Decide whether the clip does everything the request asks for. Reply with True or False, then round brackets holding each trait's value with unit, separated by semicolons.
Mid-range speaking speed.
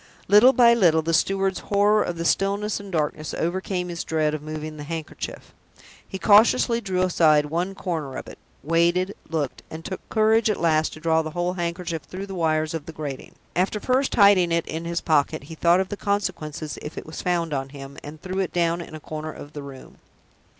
False (215 wpm)